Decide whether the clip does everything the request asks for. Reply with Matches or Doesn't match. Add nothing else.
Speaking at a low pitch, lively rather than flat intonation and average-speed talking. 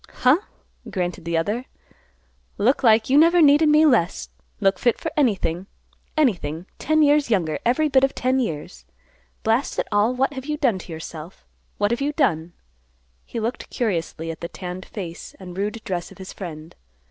Doesn't match